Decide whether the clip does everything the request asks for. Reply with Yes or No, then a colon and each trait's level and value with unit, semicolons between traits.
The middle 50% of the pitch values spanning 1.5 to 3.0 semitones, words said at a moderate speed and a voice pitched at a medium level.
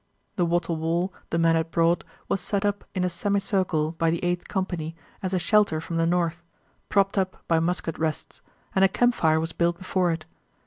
Yes: narrow, 2.4 semitones; average, 195 wpm; medium, 175 Hz